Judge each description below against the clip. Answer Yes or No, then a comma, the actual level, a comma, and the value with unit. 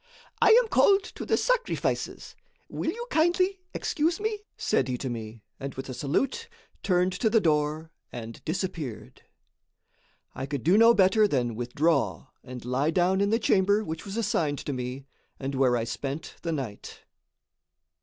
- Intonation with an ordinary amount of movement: No, wide, 8.7 semitones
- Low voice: No, medium, 160 Hz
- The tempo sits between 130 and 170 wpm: Yes, average, 165 wpm